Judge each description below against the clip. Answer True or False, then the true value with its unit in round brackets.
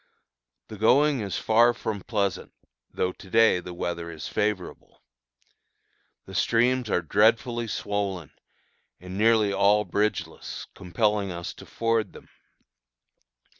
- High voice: False (105 Hz)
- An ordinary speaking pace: False (120 wpm)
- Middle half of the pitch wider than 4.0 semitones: False (3.7 semitones)